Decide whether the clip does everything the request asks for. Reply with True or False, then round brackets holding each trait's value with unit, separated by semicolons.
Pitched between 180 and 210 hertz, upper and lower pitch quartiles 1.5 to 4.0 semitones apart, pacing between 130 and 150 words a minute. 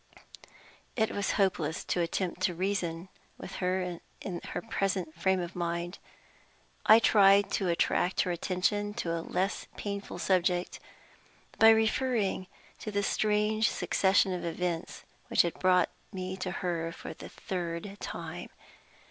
True (185 Hz; 2.6 semitones; 140 wpm)